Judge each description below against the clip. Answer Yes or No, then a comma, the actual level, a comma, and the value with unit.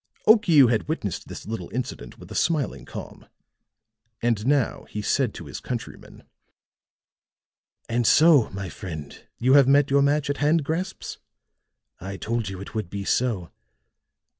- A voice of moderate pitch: No, low, 120 Hz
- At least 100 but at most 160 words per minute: Yes, average, 150 wpm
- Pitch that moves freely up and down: Yes, wide, 6.2 semitones